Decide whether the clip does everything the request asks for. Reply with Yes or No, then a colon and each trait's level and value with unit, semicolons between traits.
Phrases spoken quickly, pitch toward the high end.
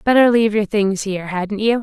Yes: fast, 230 wpm; high, 210 Hz